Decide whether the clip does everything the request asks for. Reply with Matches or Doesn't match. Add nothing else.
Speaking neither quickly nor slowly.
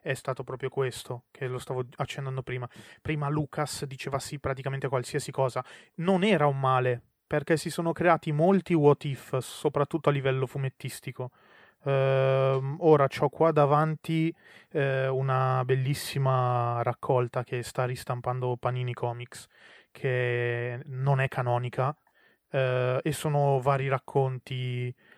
Matches